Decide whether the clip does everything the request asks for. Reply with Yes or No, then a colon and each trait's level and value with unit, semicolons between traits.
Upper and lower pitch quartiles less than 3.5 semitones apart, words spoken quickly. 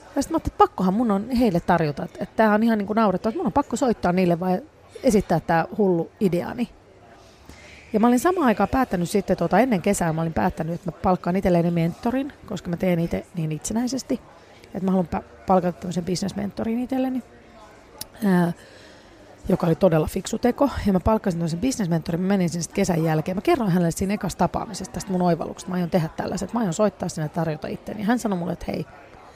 No: average, 4.2 semitones; fast, 210 wpm